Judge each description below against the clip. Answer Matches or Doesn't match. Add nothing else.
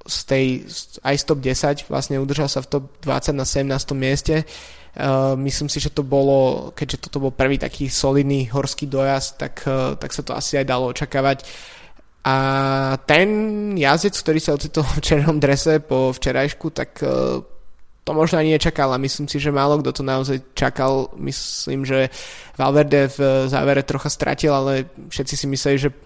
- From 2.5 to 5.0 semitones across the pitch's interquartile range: Doesn't match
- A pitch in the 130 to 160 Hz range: Matches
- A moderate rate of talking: Doesn't match